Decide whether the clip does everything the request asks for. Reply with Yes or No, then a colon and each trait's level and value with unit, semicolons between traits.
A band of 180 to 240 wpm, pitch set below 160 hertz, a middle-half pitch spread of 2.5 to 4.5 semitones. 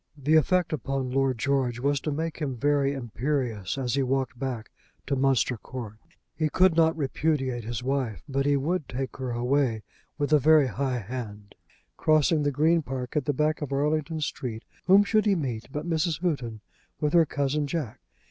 Yes: average, 185 wpm; medium, 140 Hz; average, 3.4 semitones